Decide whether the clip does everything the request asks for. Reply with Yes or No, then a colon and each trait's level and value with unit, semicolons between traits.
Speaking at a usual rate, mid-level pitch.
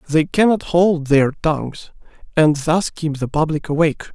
Yes: average, 160 wpm; medium, 160 Hz